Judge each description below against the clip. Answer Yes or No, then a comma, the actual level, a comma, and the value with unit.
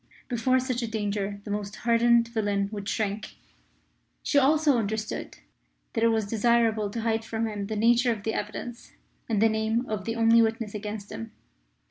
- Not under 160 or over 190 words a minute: Yes, average, 175 wpm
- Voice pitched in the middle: No, high, 220 Hz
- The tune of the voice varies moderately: No, narrow, 2.0 semitones